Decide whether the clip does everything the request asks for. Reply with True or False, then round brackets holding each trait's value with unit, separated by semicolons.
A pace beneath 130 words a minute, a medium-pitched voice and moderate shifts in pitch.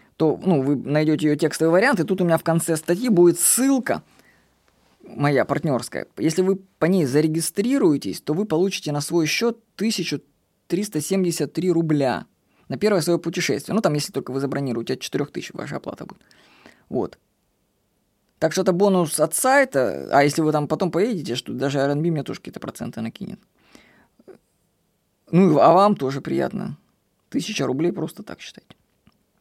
False (155 wpm; 165 Hz; 4.3 semitones)